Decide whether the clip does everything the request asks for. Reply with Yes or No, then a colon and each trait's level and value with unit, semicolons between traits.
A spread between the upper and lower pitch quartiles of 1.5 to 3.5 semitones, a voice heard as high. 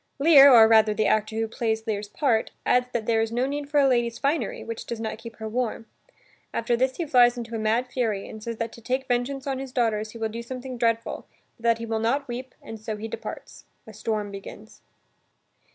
Yes: narrow, 2.4 semitones; high, 230 Hz